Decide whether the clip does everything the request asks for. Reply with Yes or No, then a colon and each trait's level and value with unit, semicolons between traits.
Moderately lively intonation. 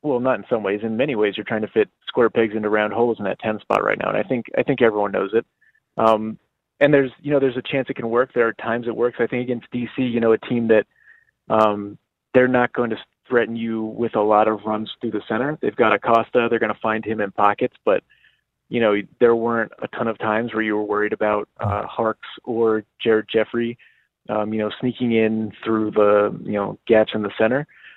No: narrow, 2.0 semitones